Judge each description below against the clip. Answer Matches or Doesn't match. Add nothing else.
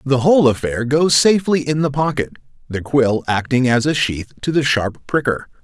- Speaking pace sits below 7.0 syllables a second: Matches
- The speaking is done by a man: Matches